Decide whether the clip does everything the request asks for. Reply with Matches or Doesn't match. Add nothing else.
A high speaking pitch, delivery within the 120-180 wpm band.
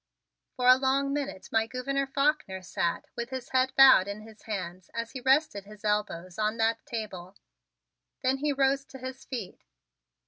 Matches